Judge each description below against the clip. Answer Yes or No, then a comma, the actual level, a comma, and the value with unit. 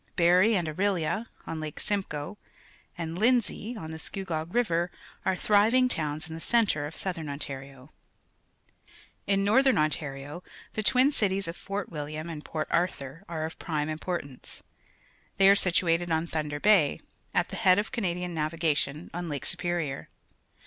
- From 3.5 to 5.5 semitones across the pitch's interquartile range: Yes, average, 4.3 semitones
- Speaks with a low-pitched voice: No, medium, 170 Hz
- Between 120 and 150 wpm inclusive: Yes, average, 145 wpm